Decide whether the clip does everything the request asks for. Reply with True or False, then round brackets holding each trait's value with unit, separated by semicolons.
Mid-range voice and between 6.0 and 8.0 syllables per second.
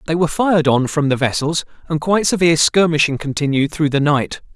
True (155 Hz; 6.2 syllables/s)